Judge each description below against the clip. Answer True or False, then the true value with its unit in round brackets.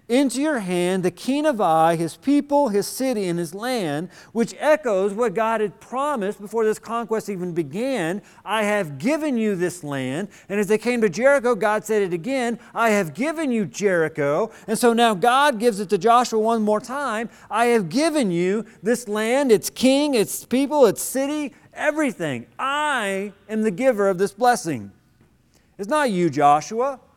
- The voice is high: True (220 Hz)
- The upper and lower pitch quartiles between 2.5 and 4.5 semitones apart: False (5.1 semitones)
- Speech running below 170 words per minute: False (180 wpm)